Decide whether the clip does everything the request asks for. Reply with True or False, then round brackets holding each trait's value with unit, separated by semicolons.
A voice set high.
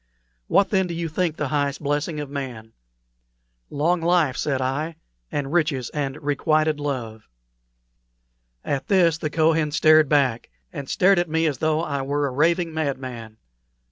False (150 Hz)